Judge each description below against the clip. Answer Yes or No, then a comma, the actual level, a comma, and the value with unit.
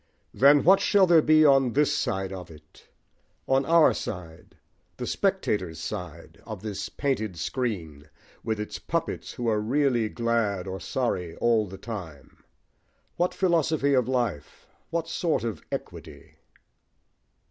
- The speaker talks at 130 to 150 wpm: Yes, slow, 135 wpm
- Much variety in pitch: Yes, wide, 7.4 semitones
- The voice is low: Yes, low, 115 Hz